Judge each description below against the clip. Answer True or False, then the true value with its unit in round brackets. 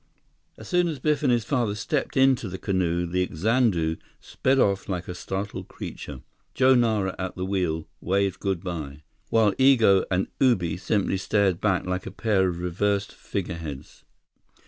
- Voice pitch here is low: True (95 Hz)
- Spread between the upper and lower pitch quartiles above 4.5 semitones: False (4.1 semitones)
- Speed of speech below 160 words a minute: False (165 wpm)